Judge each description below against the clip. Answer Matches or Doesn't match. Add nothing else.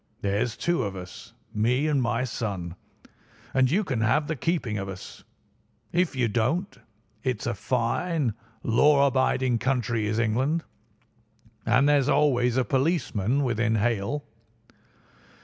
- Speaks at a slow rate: Matches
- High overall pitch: Doesn't match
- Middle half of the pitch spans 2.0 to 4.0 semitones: Doesn't match